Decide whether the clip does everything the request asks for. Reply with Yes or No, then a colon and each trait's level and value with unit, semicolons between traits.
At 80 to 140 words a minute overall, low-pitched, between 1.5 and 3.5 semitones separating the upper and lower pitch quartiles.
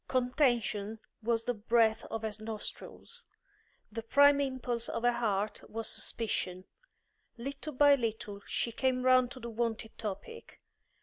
No: slow, 135 wpm; high, 235 Hz; narrow, 2.6 semitones